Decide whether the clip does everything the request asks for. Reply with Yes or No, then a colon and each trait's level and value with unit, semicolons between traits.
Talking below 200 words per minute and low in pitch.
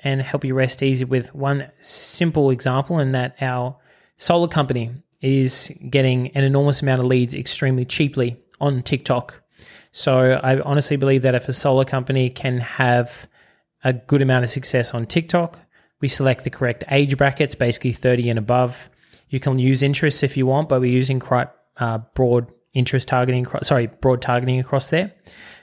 Yes: average, 170 wpm; low, 130 Hz